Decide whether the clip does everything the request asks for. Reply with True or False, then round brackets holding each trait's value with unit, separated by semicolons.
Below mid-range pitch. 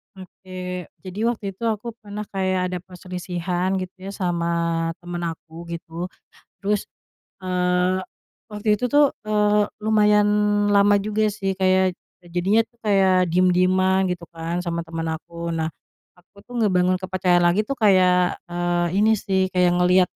False (185 Hz)